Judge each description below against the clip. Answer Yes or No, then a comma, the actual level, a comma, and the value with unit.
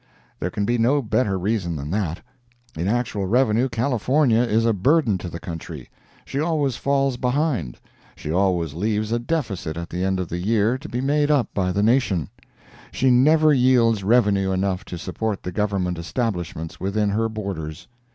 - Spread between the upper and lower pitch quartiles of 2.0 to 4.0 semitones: No, average, 5.2 semitones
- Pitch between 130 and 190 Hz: No, low, 105 Hz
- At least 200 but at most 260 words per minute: No, average, 175 wpm